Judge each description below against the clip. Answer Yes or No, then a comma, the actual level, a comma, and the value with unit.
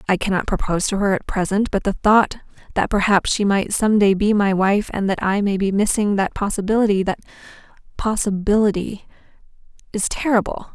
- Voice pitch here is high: Yes, high, 200 Hz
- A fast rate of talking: No, average, 170 wpm